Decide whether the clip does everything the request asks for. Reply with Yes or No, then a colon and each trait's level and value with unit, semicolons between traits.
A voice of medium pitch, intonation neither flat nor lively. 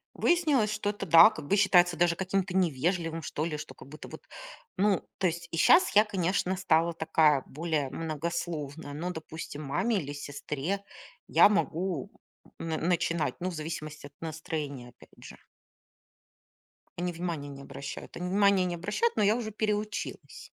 Yes: medium, 170 Hz; average, 3.9 semitones